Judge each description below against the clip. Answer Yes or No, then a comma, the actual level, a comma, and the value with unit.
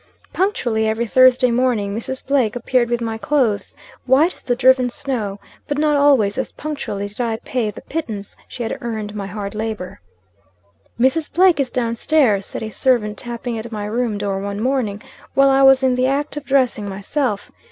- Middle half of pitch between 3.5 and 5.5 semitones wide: Yes, average, 4.0 semitones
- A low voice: No, high, 240 Hz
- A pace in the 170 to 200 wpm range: Yes, average, 185 wpm